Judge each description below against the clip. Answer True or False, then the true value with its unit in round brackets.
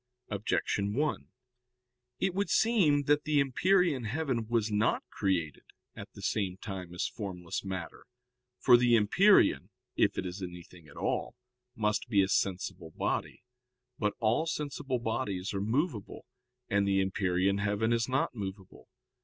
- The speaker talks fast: False (145 wpm)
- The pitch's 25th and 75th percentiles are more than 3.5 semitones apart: True (5.5 semitones)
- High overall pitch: False (105 Hz)